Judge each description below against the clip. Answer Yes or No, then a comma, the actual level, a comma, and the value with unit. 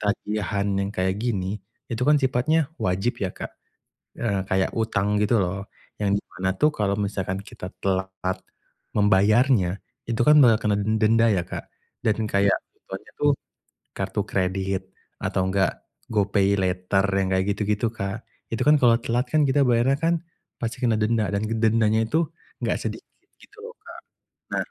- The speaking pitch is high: No, low, 105 Hz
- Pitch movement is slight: No, average, 3.1 semitones